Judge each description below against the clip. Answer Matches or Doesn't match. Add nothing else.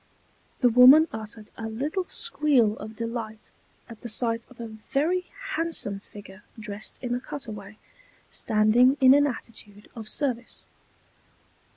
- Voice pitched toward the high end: Matches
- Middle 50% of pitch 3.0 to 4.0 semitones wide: Matches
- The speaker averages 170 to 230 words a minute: Doesn't match